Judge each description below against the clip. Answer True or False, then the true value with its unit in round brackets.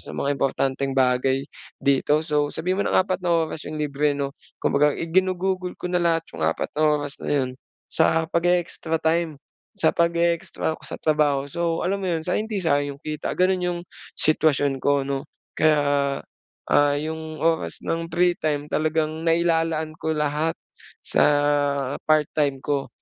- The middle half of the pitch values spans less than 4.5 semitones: True (2.8 semitones)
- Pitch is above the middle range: False (155 Hz)